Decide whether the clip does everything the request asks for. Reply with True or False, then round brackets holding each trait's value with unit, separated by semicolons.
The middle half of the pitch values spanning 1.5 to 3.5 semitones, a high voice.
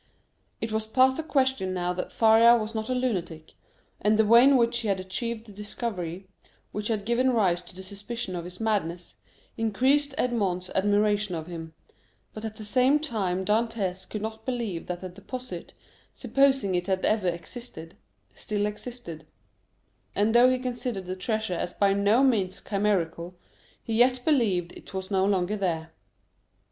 False (4.2 semitones; 210 Hz)